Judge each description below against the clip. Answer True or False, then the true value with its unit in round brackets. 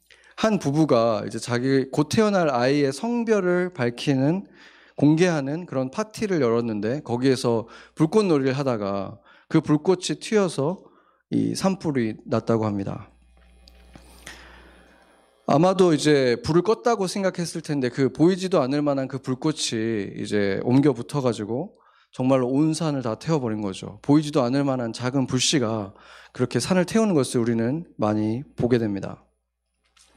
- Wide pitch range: True (6.1 semitones)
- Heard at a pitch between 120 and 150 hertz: True (135 Hz)